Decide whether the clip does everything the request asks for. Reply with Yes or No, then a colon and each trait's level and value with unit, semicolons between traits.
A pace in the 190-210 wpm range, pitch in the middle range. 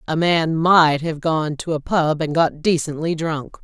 Yes: average, 200 wpm; medium, 160 Hz